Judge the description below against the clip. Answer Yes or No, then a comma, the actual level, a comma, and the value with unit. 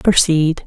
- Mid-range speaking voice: Yes, medium, 165 Hz